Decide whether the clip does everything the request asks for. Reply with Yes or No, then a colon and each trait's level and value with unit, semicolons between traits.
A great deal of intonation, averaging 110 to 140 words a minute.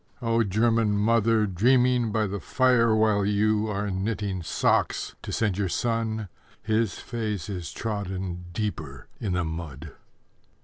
No: average, 3.1 semitones; slow, 135 wpm